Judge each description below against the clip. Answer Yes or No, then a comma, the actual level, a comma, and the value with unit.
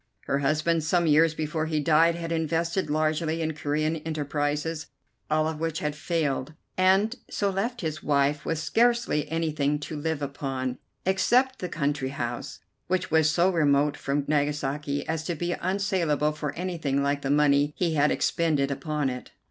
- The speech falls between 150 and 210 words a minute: Yes, average, 165 wpm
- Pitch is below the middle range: No, medium, 155 Hz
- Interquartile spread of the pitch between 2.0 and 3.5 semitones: Yes, narrow, 2.4 semitones